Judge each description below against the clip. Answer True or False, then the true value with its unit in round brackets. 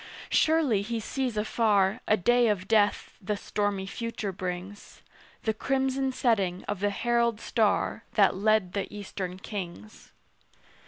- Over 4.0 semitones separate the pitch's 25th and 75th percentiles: False (3.3 semitones)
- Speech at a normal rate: False (130 wpm)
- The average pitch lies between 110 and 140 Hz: False (210 Hz)